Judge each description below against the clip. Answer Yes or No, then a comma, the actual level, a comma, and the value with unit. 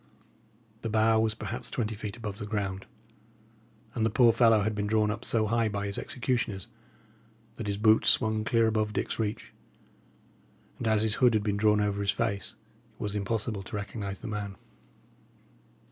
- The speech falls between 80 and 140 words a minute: No, average, 175 wpm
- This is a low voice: Yes, low, 110 Hz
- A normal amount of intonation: No, narrow, 1.5 semitones